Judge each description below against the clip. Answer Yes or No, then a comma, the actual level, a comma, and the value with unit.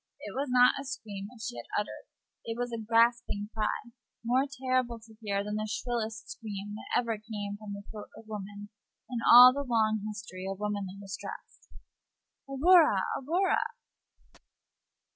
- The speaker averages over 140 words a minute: Yes, average, 160 wpm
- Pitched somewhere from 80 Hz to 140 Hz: No, high, 220 Hz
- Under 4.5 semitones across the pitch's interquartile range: Yes, average, 3.0 semitones